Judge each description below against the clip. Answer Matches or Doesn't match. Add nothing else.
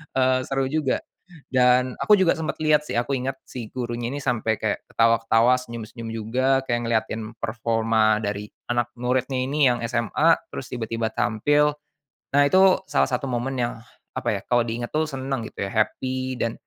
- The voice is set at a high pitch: Doesn't match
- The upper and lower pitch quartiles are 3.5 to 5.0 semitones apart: Doesn't match